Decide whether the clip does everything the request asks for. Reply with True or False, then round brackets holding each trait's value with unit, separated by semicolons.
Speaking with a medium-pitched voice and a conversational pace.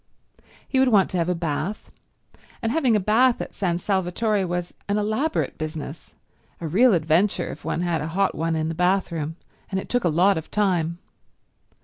True (180 Hz; 190 wpm)